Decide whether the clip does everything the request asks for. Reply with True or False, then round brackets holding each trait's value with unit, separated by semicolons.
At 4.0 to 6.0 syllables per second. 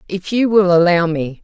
True (4.8 syllables/s)